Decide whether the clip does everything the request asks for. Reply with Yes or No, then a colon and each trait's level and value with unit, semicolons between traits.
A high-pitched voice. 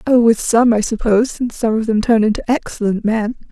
Yes: high, 225 Hz